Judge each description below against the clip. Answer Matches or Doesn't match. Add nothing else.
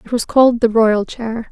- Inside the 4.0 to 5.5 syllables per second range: Matches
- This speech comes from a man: Doesn't match